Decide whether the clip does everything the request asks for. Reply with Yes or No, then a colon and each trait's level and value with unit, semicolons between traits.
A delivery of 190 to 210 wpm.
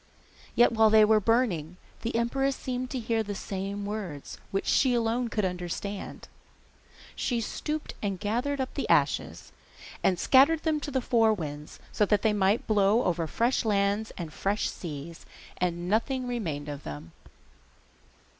No: average, 160 wpm